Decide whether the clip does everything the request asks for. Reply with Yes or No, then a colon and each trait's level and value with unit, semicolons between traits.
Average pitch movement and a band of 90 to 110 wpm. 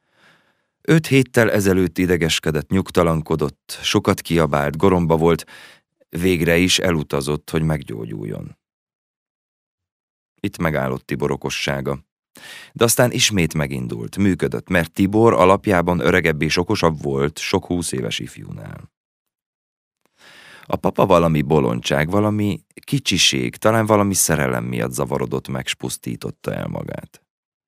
Yes: average, 4.5 semitones; slow, 105 wpm